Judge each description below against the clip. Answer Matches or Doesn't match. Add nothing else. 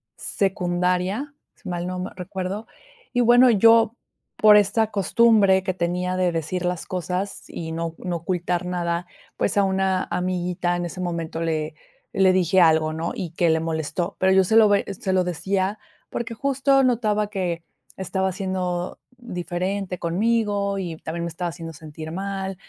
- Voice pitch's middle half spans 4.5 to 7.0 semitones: Doesn't match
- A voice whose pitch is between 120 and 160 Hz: Doesn't match